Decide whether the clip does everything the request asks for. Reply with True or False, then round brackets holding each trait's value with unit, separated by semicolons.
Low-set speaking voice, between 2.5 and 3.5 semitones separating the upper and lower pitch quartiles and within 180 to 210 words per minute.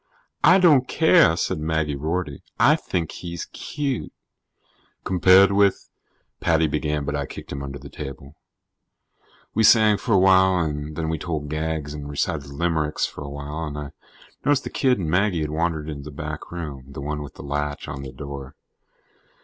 False (75 Hz; 4.0 semitones; 185 wpm)